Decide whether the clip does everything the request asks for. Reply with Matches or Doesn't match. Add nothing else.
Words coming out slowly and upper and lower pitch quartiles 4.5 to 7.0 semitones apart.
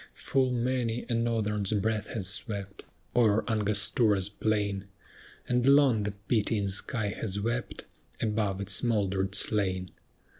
Doesn't match